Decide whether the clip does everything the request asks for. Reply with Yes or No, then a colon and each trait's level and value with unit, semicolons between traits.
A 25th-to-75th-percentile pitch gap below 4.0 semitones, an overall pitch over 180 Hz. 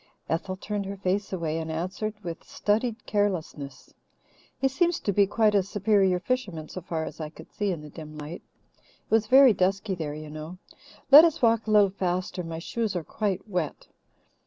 No: average, 4.4 semitones; high, 190 Hz